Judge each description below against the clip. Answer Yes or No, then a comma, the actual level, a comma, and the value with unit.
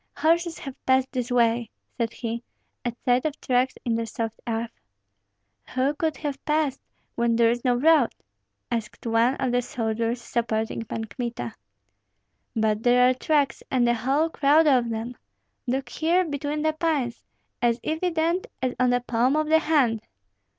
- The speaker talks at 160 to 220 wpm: Yes, average, 165 wpm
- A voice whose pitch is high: Yes, very high, 250 Hz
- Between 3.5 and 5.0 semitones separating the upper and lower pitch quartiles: Yes, average, 4.1 semitones